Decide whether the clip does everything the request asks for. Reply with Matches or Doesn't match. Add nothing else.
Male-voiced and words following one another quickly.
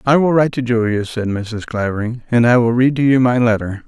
Matches